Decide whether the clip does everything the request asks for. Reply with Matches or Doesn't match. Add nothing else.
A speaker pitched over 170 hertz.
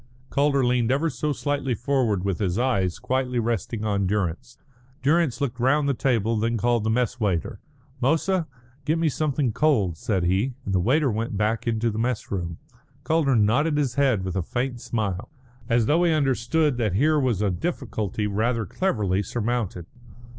Doesn't match